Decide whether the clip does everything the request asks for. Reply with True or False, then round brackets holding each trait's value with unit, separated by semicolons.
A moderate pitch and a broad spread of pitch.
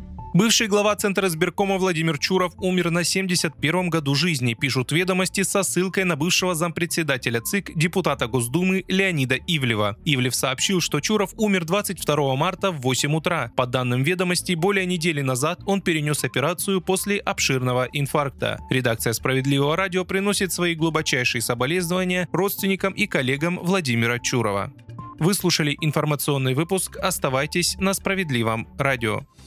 True (170 Hz; 5.9 semitones)